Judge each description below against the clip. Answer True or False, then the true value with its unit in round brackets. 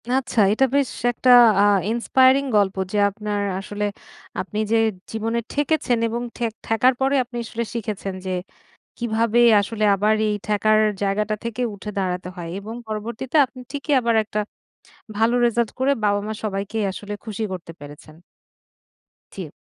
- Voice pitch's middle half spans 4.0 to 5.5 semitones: False (2.7 semitones)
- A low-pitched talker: False (220 Hz)